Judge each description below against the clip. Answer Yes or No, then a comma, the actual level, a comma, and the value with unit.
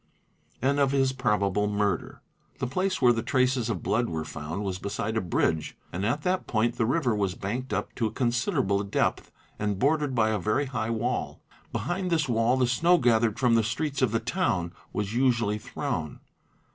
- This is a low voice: Yes, low, 120 Hz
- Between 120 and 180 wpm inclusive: No, average, 195 wpm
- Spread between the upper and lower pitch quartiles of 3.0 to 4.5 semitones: Yes, average, 4.1 semitones